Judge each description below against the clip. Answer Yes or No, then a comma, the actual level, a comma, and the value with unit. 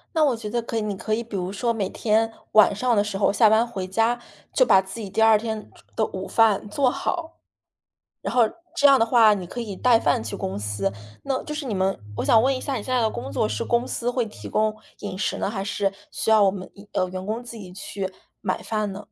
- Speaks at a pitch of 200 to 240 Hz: Yes, high, 215 Hz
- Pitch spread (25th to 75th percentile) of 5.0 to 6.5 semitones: No, average, 3.4 semitones